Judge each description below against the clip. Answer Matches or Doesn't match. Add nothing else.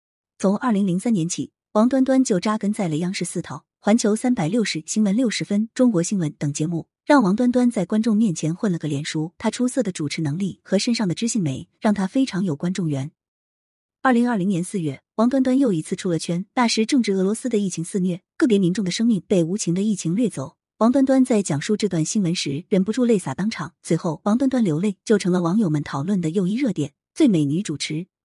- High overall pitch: Matches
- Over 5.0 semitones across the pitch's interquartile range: Matches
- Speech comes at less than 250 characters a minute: Doesn't match